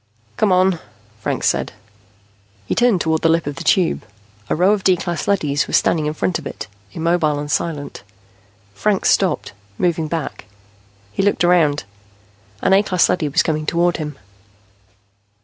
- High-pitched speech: No, medium, 170 Hz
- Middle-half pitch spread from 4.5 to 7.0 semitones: No, average, 3.3 semitones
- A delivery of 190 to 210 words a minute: No, average, 165 wpm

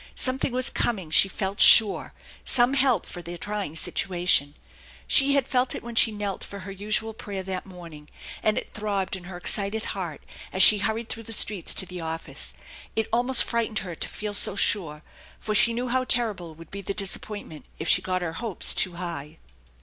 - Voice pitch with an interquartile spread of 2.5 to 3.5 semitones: No, average, 4.1 semitones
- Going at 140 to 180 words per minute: No, average, 200 wpm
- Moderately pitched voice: No, high, 200 Hz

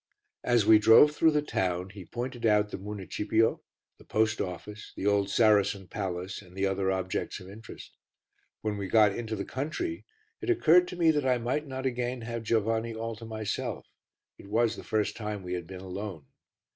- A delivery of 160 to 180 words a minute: No, average, 190 wpm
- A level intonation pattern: No, average, 3.6 semitones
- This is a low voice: Yes, low, 110 Hz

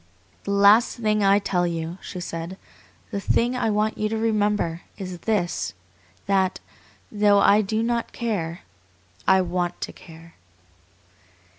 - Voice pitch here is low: No, high, 200 Hz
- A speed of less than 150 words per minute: Yes, average, 140 wpm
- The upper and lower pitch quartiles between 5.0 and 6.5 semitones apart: No, average, 3.3 semitones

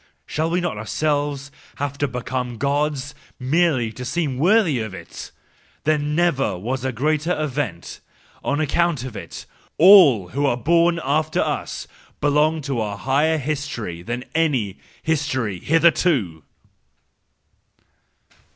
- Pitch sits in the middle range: Yes, medium, 145 Hz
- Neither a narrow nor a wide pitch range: Yes, average, 4.1 semitones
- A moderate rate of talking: No, slow, 130 wpm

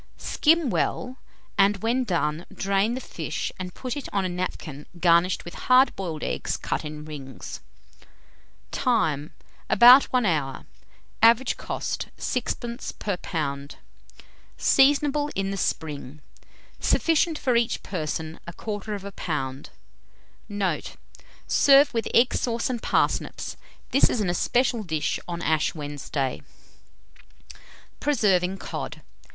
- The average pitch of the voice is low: No, high, 195 Hz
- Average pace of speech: No, slow, 120 wpm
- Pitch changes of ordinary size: No, wide, 7.6 semitones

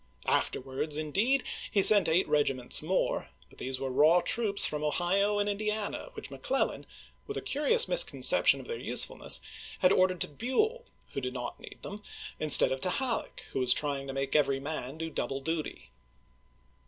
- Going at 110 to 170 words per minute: Yes, average, 165 wpm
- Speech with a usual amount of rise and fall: No, wide, 7.3 semitones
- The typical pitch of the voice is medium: Yes, medium, 165 Hz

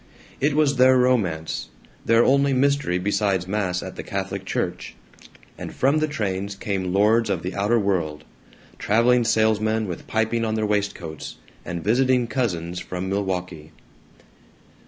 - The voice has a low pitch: Yes, low, 105 Hz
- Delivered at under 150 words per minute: Yes, average, 140 wpm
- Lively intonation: No, average, 4.8 semitones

